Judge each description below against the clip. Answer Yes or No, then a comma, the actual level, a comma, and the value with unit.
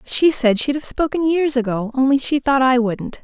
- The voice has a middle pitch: No, very high, 265 Hz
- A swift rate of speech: Yes, fast, 225 wpm